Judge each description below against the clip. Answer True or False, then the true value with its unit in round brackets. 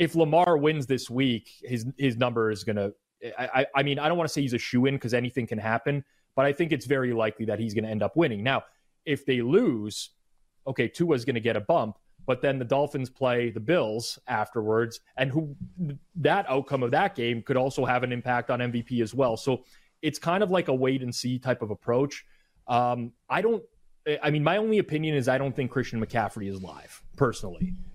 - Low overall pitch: True (130 Hz)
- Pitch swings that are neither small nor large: True (3.3 semitones)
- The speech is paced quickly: True (215 wpm)